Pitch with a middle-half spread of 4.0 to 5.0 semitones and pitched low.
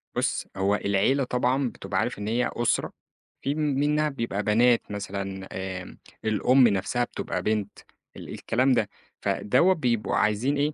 Yes: average, 4.7 semitones; low, 115 Hz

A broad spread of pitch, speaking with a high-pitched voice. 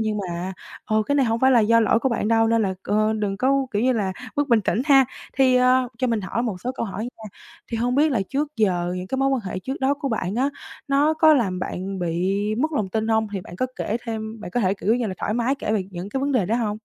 No: average, 4.2 semitones; high, 225 Hz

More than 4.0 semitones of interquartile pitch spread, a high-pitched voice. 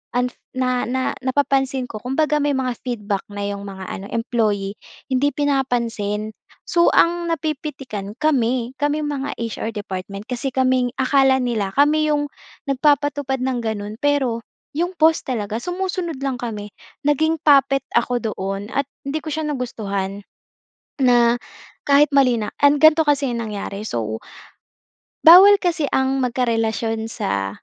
Yes: average, 4.7 semitones; very high, 255 Hz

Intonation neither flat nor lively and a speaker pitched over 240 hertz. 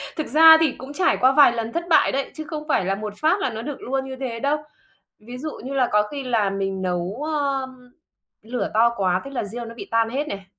Yes: average, 4.7 semitones; very high, 255 Hz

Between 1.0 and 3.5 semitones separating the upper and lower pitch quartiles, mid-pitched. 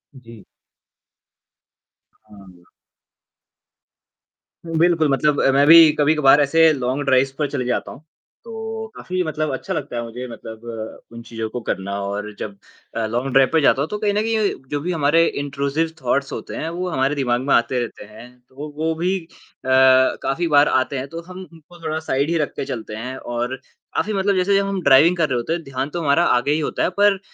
No: average, 4.7 semitones; medium, 145 Hz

